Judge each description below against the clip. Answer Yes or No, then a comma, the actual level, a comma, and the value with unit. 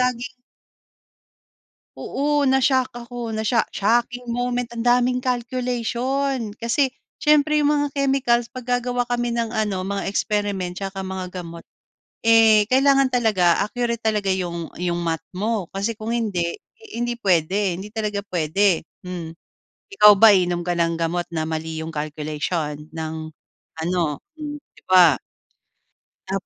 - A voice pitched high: Yes, high, 215 Hz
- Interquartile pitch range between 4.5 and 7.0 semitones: Yes, wide, 5.5 semitones